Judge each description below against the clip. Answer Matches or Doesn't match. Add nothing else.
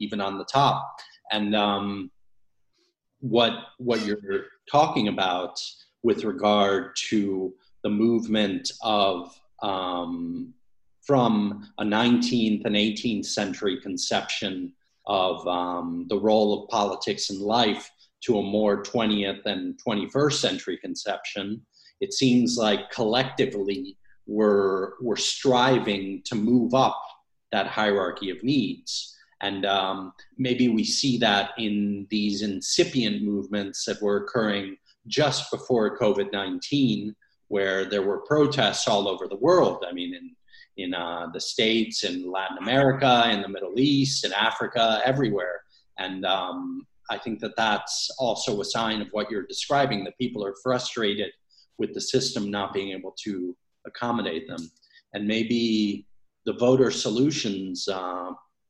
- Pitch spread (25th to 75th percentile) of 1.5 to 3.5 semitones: Doesn't match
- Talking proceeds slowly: Matches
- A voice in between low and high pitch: Doesn't match